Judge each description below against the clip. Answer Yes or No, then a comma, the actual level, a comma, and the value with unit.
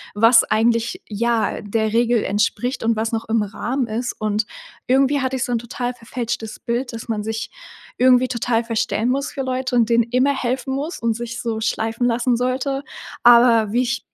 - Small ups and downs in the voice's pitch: Yes, narrow, 2.0 semitones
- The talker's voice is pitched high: Yes, high, 235 Hz